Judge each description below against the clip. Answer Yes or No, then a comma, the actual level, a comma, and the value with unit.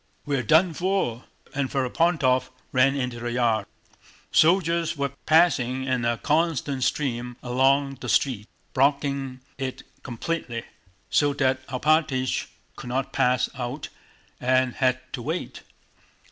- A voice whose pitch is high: No, low, 130 Hz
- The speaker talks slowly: Yes, slow, 120 wpm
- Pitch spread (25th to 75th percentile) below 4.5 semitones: Yes, average, 2.8 semitones